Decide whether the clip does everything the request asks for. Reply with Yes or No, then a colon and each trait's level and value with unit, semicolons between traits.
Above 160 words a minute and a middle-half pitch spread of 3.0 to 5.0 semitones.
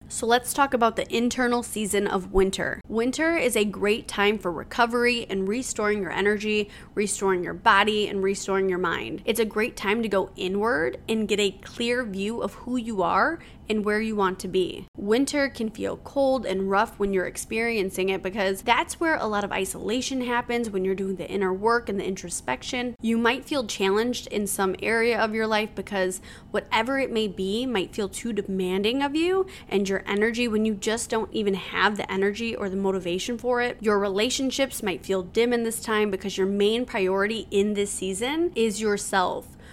Yes: average, 195 wpm; average, 3.4 semitones